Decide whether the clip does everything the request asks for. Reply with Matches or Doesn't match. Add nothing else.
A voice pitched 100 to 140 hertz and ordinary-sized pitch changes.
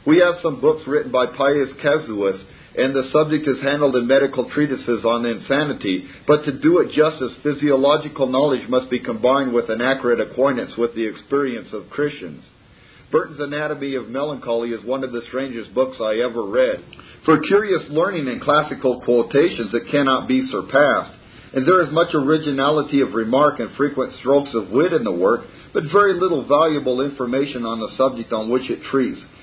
Matches